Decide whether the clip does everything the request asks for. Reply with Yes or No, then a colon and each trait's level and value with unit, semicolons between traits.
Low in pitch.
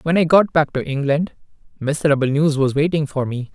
No: medium, 150 Hz